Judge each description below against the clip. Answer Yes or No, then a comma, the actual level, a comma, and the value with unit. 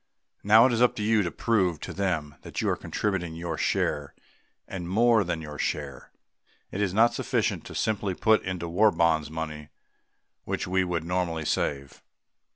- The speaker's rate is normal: Yes, average, 180 wpm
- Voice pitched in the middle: No, very low, 90 Hz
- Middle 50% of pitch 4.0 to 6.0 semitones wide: Yes, average, 4.5 semitones